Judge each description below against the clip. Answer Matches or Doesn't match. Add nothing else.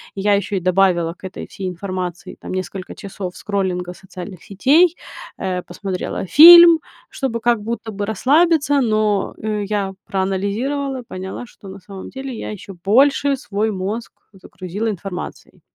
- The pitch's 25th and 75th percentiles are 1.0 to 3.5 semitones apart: Doesn't match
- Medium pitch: Doesn't match